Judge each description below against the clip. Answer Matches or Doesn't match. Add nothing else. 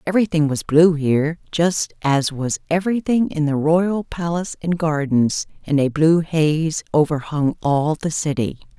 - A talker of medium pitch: Matches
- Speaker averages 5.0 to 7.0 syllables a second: Doesn't match